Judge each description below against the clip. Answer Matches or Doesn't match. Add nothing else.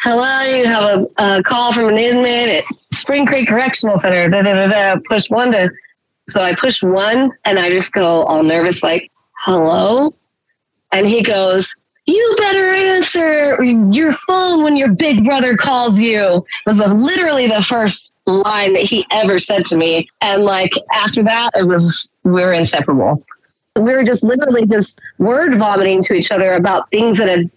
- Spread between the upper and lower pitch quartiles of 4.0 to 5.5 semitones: Matches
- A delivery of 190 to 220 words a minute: Doesn't match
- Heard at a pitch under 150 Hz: Doesn't match